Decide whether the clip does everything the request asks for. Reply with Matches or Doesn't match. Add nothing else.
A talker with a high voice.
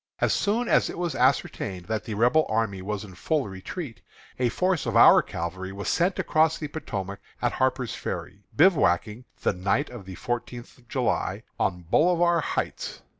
Doesn't match